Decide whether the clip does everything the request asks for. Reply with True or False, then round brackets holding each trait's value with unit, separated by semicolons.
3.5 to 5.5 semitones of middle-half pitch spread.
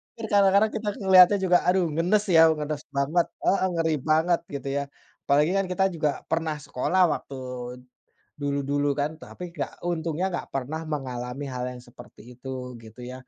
True (4.4 semitones)